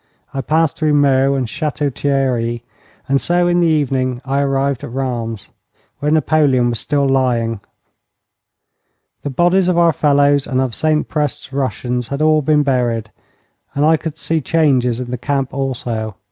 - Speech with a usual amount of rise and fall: Yes, average, 3.3 semitones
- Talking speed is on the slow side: No, average, 160 wpm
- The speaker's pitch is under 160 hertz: Yes, low, 135 Hz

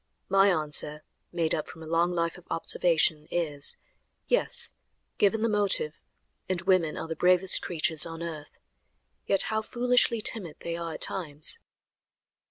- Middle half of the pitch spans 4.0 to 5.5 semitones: No, average, 3.4 semitones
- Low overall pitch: No, medium, 170 Hz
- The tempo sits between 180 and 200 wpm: No, average, 150 wpm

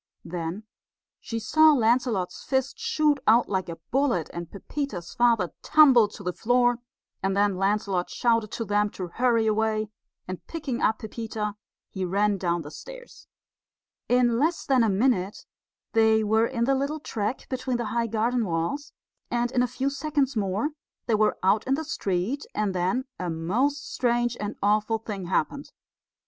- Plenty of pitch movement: No, average, 4.5 semitones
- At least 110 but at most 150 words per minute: No, average, 165 wpm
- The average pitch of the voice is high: Yes, high, 225 Hz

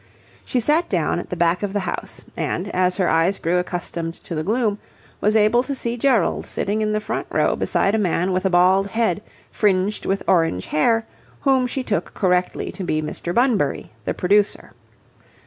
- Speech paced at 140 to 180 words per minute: No, average, 190 wpm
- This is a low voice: No, high, 195 Hz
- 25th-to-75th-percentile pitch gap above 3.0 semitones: Yes, average, 3.8 semitones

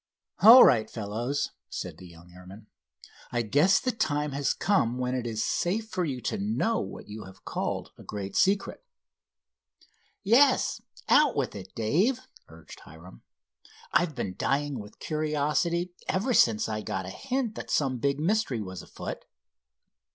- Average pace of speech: Yes, average, 155 wpm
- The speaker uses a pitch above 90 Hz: Yes, medium, 140 Hz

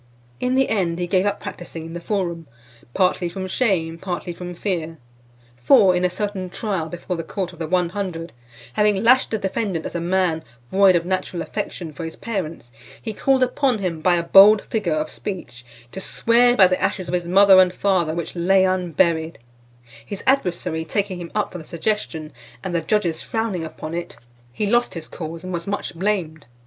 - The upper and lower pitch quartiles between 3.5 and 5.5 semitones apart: No, average, 3.1 semitones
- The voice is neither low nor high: Yes, medium, 180 Hz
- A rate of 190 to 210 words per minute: Yes, average, 195 wpm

